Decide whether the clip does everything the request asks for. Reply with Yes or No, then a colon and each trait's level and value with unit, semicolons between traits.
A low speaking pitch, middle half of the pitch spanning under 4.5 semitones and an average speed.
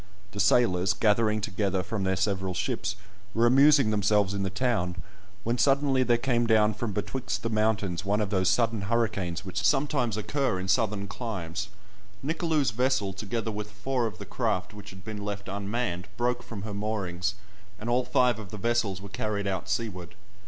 Yes: low, 105 Hz; average, 3.4 semitones; average, 180 wpm